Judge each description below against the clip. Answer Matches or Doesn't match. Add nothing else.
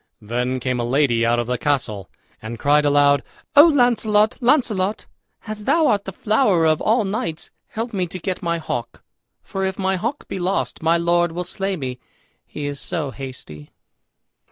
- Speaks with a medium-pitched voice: Matches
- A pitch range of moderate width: Doesn't match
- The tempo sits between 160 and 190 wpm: Matches